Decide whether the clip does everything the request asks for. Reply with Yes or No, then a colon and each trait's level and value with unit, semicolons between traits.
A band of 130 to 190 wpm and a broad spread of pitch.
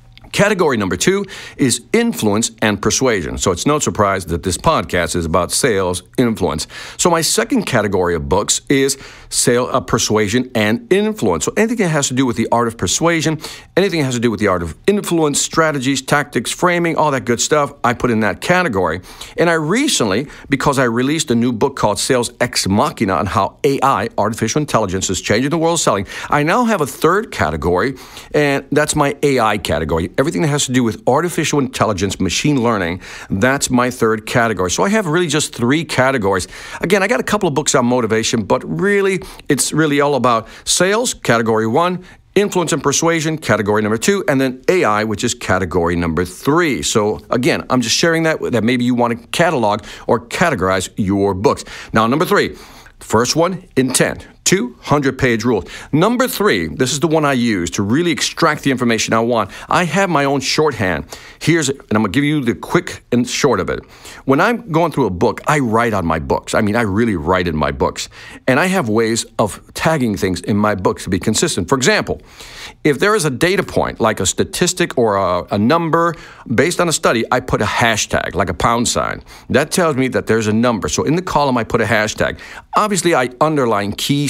No: fast, 205 wpm; wide, 6.3 semitones